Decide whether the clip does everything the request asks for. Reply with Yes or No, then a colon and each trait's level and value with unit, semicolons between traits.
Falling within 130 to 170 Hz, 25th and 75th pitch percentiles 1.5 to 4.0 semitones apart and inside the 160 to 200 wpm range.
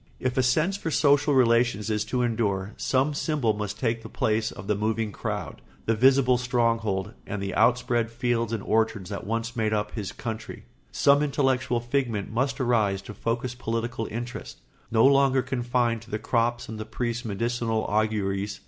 No: low, 115 Hz; narrow, 2.5 semitones; average, 175 wpm